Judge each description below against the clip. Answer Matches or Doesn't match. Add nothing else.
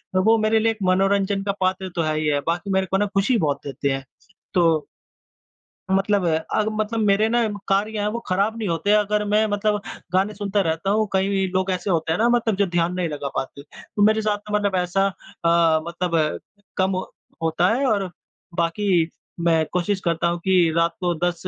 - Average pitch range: Matches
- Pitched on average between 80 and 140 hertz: Doesn't match